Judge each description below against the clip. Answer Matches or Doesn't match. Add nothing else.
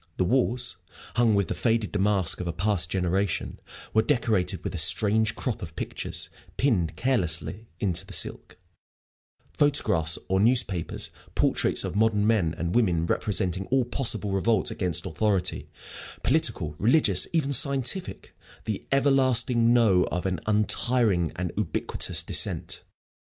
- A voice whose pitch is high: Doesn't match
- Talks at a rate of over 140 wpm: Doesn't match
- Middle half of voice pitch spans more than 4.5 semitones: Matches